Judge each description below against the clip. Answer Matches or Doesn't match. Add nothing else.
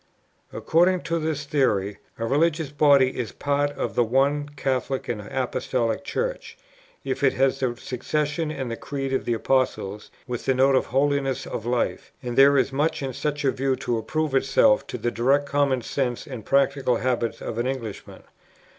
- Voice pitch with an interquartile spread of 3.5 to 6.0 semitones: Doesn't match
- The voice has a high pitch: Doesn't match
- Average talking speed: Matches